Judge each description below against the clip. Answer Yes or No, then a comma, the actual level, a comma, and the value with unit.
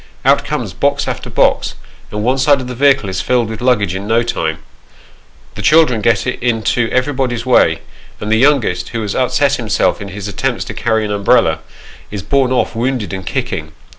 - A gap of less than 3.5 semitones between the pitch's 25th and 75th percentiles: No, average, 3.8 semitones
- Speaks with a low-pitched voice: Yes, low, 115 Hz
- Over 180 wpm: Yes, average, 190 wpm